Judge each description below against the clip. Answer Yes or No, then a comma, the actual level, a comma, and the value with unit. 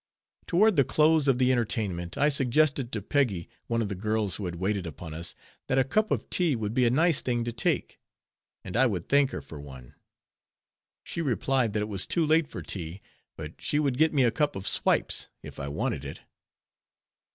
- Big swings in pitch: Yes, wide, 6.8 semitones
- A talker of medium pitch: No, low, 120 Hz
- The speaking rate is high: Yes, fast, 210 wpm